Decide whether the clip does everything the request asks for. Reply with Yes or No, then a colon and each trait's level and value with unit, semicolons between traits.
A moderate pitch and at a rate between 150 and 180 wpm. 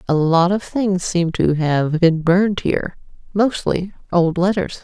Yes: medium, 175 Hz; average, 160 wpm